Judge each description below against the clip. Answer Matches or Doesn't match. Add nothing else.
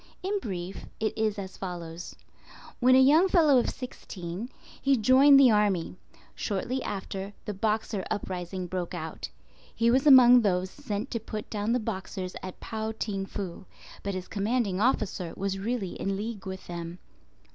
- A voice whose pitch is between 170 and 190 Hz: Doesn't match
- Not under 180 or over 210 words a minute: Doesn't match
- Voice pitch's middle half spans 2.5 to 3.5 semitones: Doesn't match